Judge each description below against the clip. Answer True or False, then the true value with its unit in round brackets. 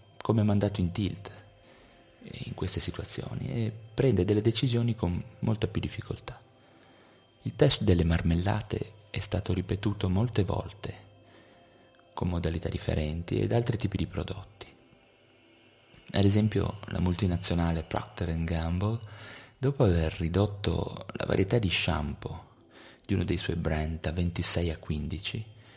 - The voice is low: True (100 Hz)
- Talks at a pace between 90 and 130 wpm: True (125 wpm)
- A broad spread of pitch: False (4.4 semitones)